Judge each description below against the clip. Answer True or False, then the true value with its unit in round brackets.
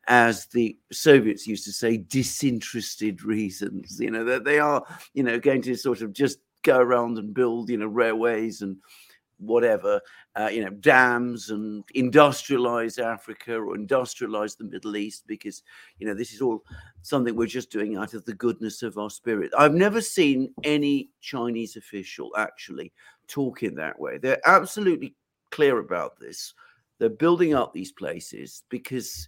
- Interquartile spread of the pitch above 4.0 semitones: True (4.8 semitones)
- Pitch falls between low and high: False (120 Hz)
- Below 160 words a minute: False (165 wpm)